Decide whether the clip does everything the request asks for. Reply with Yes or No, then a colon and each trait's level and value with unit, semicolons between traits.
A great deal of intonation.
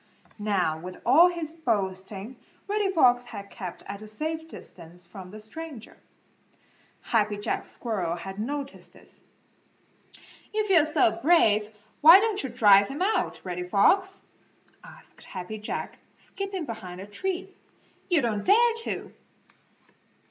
Yes: wide, 9.0 semitones